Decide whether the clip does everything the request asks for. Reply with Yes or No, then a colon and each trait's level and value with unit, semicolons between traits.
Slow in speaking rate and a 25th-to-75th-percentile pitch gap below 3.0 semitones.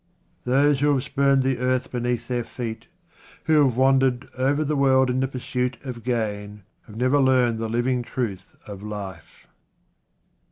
No: average, 160 wpm; narrow, 2.4 semitones